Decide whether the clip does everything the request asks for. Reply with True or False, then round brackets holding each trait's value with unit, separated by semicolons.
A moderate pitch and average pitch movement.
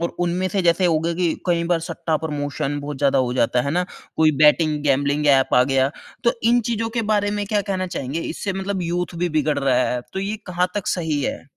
True (165 Hz; 4.4 semitones)